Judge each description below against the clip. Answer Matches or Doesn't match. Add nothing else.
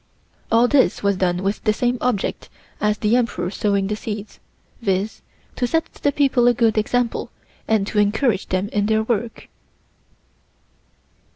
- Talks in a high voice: Matches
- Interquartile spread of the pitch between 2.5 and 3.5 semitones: Matches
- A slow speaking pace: Doesn't match